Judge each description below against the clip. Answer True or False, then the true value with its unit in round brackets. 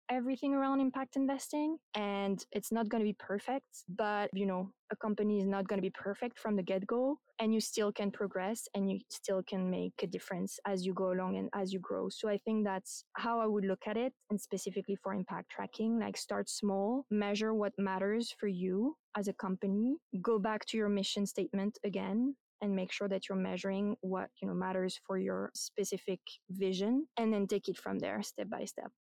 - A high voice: True (205 Hz)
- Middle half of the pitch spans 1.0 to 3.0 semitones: True (2.7 semitones)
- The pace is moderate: False (210 wpm)